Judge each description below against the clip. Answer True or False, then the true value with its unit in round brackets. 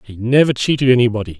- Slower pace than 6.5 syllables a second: False (7.2 syllables/s)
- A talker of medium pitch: False (120 Hz)